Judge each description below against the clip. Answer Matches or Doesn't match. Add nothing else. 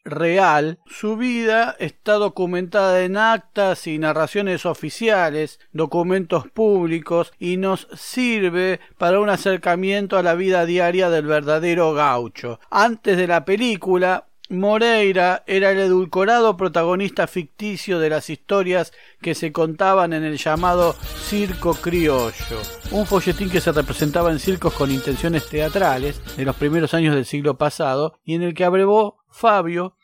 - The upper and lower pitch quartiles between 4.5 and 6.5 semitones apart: Doesn't match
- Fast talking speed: Doesn't match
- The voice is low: Doesn't match